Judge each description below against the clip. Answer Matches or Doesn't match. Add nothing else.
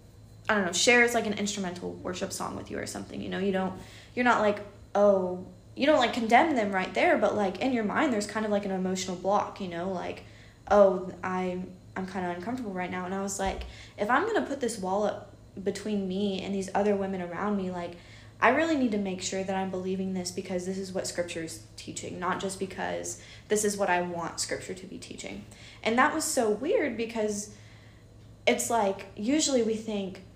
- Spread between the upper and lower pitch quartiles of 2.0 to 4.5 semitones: Matches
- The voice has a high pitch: Matches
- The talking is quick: Matches